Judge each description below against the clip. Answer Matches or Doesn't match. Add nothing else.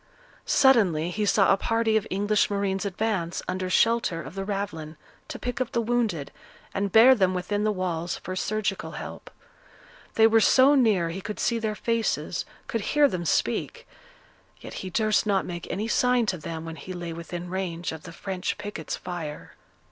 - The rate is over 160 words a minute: Matches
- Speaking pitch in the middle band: Doesn't match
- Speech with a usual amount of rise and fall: Matches